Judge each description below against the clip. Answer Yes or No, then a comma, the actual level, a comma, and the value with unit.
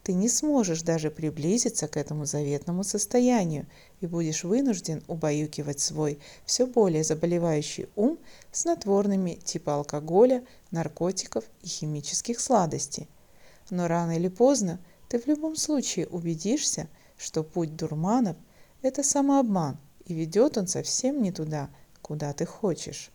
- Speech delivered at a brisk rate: No, average, 125 wpm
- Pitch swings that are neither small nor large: No, wide, 6.8 semitones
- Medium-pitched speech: Yes, medium, 175 Hz